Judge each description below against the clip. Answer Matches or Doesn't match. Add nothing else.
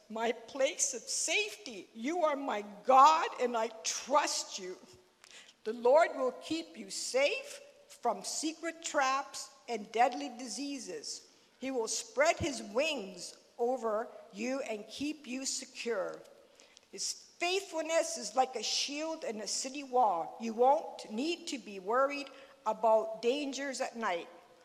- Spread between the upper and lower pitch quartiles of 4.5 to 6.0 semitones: Matches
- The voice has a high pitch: Matches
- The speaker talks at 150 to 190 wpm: Doesn't match